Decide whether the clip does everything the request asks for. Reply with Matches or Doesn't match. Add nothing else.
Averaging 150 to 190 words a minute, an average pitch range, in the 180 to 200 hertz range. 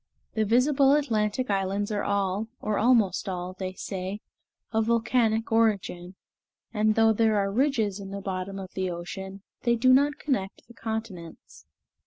Doesn't match